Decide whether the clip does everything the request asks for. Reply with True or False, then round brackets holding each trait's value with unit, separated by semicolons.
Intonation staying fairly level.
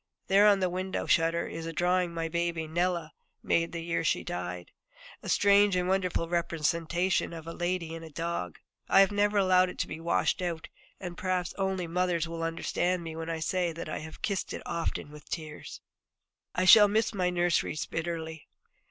True (2.0 semitones)